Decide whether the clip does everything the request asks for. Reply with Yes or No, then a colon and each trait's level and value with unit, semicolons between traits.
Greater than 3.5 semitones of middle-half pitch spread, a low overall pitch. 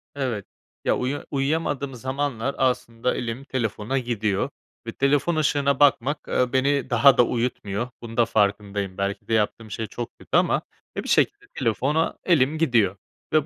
Yes: average, 3.9 semitones; low, 125 Hz